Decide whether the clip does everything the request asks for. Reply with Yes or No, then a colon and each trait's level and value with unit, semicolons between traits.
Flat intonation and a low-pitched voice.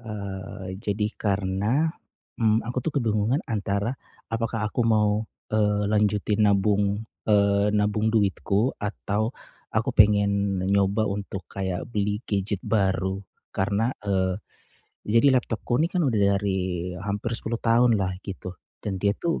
Yes: narrow, 2.0 semitones; low, 105 Hz